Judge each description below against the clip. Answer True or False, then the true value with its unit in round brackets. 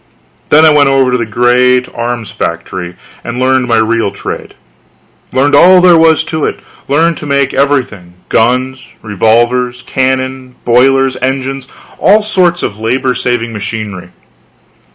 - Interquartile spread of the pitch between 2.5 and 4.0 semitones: True (3.0 semitones)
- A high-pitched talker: False (130 Hz)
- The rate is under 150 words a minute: True (140 wpm)